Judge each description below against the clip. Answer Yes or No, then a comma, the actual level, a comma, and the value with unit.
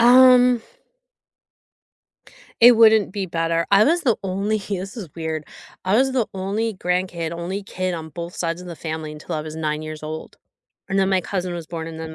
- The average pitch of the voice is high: No, medium, 180 Hz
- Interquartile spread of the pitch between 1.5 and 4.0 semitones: No, average, 4.4 semitones